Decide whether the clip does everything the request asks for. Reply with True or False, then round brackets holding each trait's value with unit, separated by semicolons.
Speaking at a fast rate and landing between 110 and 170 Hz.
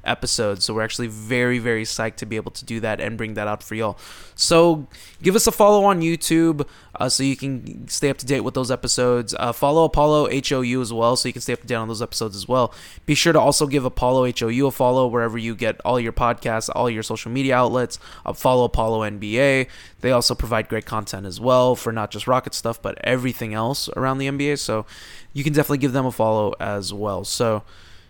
True (230 wpm; 120 Hz)